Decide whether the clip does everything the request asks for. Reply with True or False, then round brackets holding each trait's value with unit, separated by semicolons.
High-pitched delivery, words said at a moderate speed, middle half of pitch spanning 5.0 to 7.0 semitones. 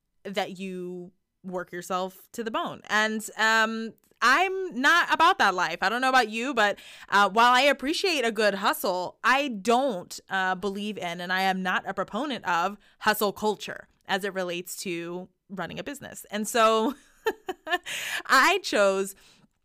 True (210 Hz; 160 wpm; 5.6 semitones)